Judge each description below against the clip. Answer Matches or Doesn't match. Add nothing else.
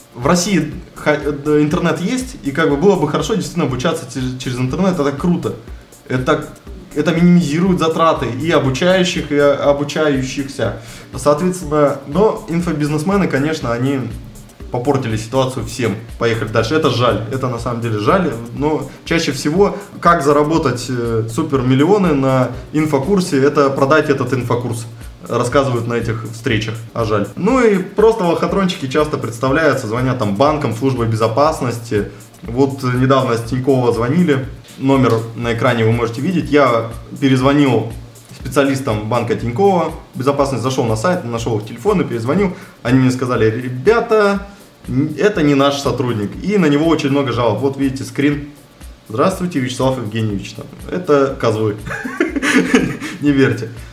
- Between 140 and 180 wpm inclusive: Doesn't match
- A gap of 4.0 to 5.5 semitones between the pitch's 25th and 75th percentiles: Matches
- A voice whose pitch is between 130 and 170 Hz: Matches